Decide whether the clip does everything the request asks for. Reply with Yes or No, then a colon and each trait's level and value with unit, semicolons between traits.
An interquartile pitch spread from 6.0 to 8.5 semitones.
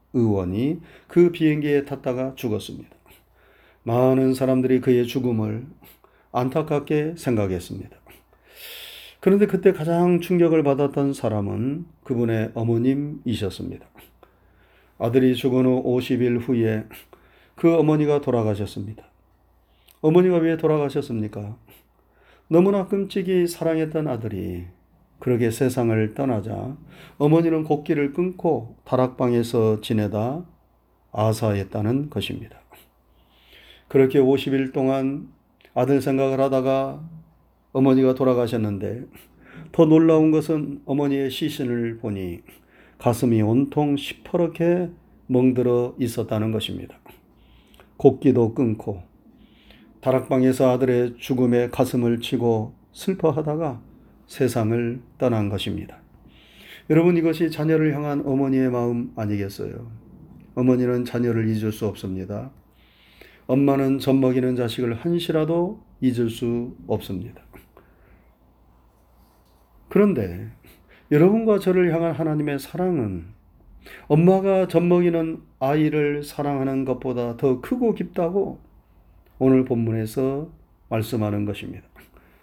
No: average, 5.2 semitones